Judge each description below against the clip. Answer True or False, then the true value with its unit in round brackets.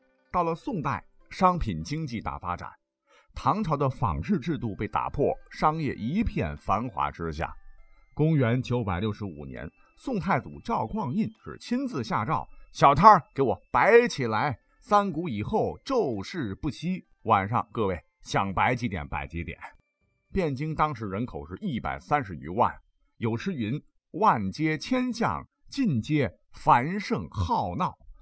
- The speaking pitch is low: True (125 Hz)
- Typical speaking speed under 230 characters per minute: True (205 characters per minute)